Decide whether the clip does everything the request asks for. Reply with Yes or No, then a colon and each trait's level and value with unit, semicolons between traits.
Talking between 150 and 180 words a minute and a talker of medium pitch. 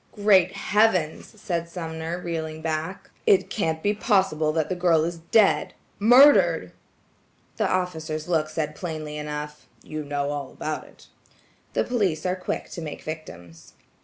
No: slow, 135 wpm; medium, 160 Hz